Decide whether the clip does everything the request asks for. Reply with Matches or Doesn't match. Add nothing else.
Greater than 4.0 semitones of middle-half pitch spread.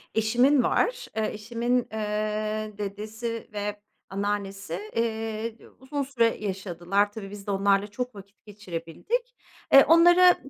Doesn't match